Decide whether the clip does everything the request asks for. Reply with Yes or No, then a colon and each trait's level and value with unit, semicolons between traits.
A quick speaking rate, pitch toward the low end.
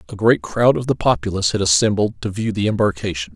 Yes: fast, 215 wpm; low, 100 Hz